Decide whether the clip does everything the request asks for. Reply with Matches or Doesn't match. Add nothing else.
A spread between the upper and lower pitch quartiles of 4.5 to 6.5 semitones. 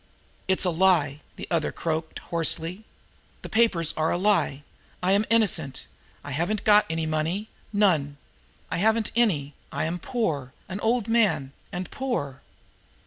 Matches